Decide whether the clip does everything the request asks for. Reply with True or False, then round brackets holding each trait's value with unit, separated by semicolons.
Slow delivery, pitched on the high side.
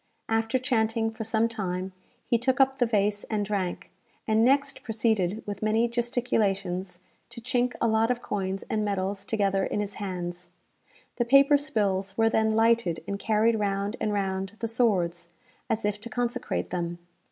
False (165 wpm; 215 Hz)